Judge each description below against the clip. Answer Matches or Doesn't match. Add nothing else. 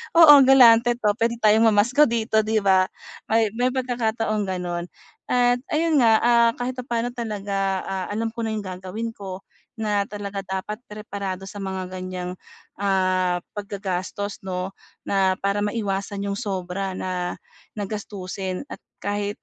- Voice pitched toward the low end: Doesn't match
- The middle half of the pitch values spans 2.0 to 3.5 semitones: Matches